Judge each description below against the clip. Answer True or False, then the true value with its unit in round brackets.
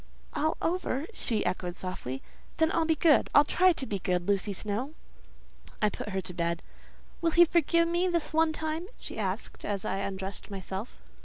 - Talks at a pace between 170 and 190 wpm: True (180 wpm)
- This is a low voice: False (245 Hz)